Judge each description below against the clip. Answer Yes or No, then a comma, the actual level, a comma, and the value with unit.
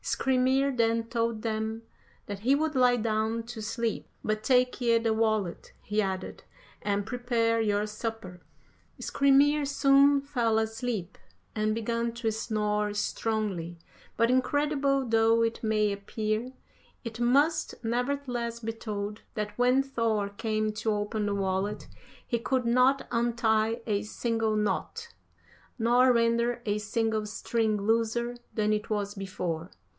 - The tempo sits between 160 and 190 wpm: No, slow, 135 wpm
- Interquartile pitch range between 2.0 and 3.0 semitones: Yes, narrow, 2.4 semitones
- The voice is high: Yes, high, 225 Hz